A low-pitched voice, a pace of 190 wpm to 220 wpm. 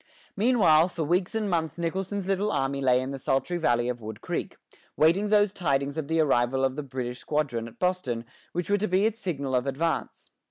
No: medium, 155 Hz; fast, 205 wpm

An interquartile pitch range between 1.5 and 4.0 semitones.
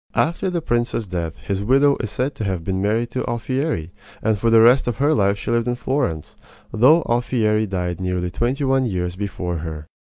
No: wide, 5.5 semitones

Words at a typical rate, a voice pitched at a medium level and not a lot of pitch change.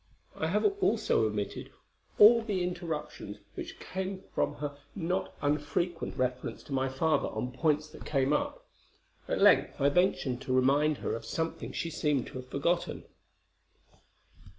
No: average, 150 wpm; medium, 150 Hz; average, 4.9 semitones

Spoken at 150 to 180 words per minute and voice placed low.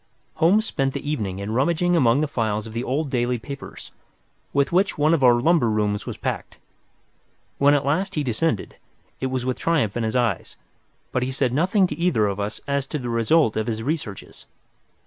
No: average, 200 wpm; low, 130 Hz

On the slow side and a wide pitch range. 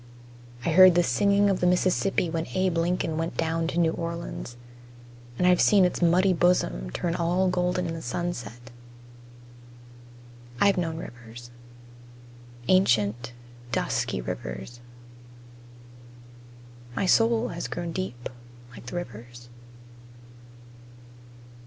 Yes: slow, 115 wpm; wide, 6.9 semitones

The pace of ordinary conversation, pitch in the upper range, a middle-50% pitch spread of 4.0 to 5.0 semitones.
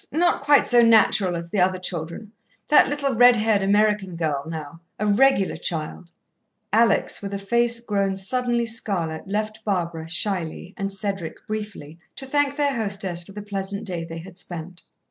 Yes: average, 170 wpm; high, 200 Hz; average, 4.4 semitones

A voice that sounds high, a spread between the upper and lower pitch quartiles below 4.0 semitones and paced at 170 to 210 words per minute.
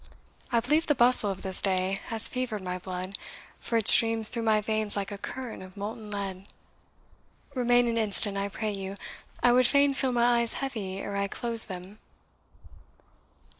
Yes: high, 215 Hz; average, 3.4 semitones; average, 175 wpm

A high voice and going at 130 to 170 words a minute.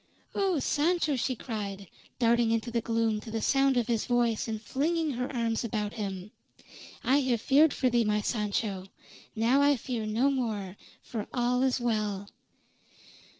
Yes: high, 235 Hz; average, 160 wpm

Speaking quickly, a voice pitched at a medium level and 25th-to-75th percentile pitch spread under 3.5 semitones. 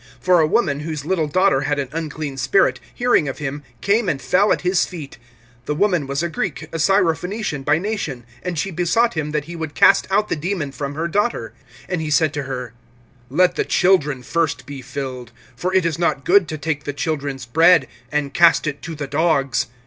No: fast, 210 wpm; medium, 155 Hz; average, 4.2 semitones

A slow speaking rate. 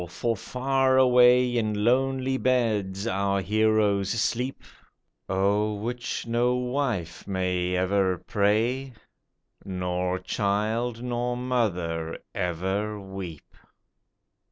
Yes: slow, 90 wpm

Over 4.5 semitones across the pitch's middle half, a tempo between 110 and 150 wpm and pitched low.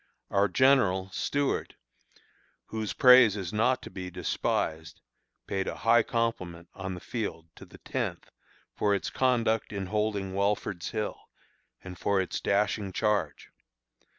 No: average, 3.2 semitones; slow, 135 wpm; low, 100 Hz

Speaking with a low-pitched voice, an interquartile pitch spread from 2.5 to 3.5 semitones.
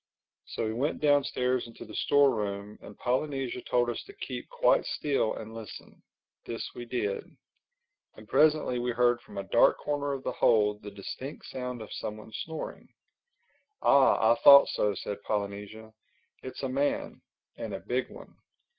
No: low, 120 Hz; average, 4.4 semitones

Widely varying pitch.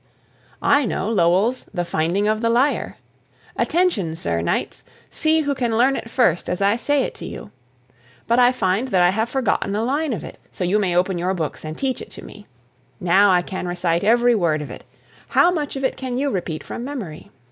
Yes: wide, 6.4 semitones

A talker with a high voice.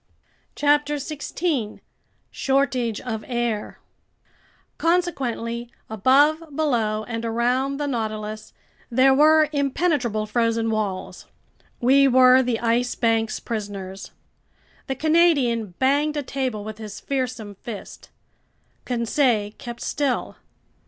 Yes: high, 245 Hz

